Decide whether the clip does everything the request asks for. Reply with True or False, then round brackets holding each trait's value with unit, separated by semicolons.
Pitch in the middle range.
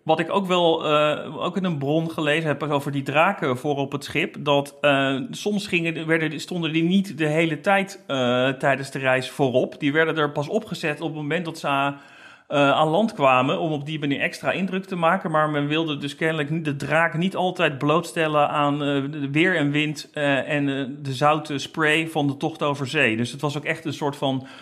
True (150 Hz)